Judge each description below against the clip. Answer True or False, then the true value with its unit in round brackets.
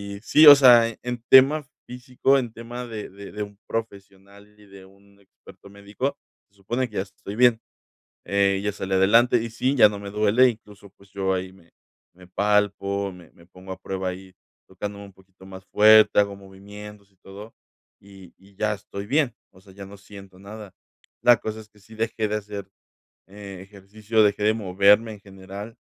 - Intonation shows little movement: True (2.2 semitones)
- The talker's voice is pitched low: True (100 Hz)